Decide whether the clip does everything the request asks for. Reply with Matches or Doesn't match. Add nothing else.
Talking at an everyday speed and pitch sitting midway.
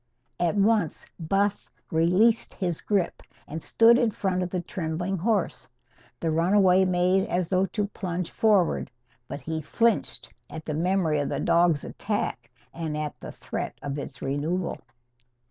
Matches